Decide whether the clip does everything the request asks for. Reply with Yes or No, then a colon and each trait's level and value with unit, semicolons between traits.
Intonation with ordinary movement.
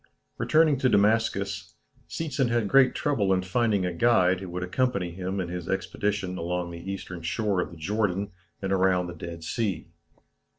Yes: average, 3.8 semitones